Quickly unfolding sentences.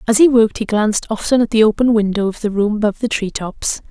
Yes: fast, 260 wpm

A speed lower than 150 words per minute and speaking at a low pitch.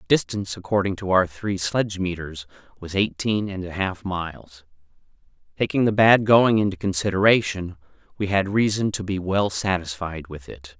No: average, 160 wpm; very low, 95 Hz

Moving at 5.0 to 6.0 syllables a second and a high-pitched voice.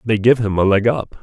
No: 5.4 syllables/s; low, 110 Hz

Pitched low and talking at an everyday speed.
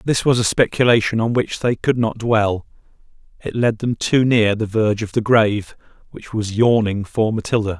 Yes: low, 110 Hz; average, 185 wpm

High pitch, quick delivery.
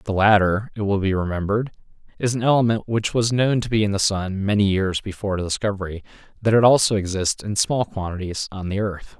No: low, 100 Hz; fast, 210 wpm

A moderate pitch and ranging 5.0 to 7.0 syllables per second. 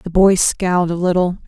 Yes: medium, 180 Hz; 5.2 syllables/s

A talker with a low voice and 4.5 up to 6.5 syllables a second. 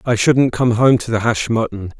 Yes: low, 115 Hz; 5.0 syllables/s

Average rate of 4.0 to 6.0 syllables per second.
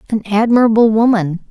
Yes: 5.8 syllables/s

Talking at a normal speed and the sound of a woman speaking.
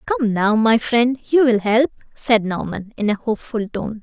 Yes: average, 180 wpm; female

